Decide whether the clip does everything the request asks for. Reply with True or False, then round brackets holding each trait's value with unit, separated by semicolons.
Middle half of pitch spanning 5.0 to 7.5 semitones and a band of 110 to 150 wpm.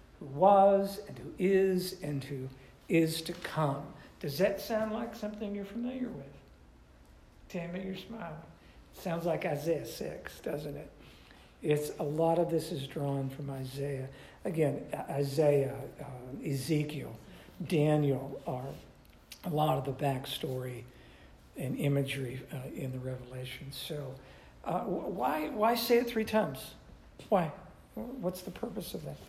True (5.5 semitones; 140 wpm)